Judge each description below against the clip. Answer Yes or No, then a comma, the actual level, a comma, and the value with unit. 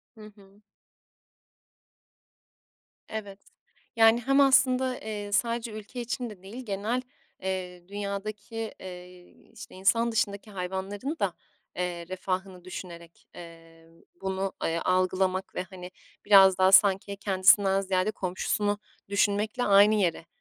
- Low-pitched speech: No, high, 195 Hz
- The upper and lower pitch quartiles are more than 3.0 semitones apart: No, narrow, 2.6 semitones